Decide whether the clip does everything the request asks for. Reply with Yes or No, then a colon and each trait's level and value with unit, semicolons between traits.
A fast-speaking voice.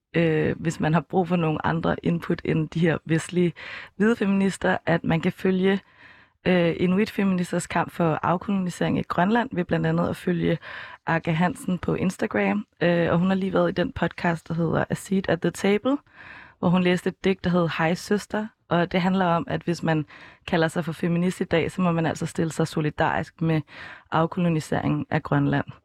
No: average, 200 wpm